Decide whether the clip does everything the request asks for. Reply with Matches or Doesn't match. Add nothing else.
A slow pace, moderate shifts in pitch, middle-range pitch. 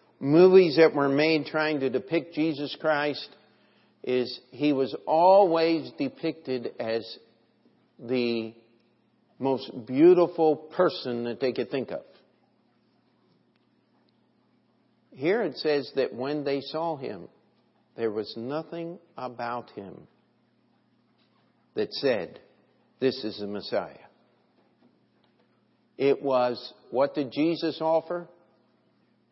Matches